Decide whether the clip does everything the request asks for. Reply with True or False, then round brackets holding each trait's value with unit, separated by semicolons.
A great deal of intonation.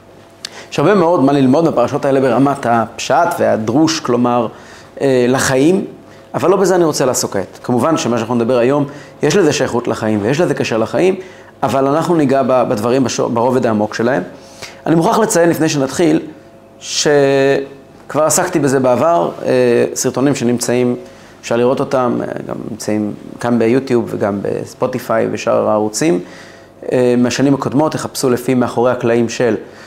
False (3.3 semitones)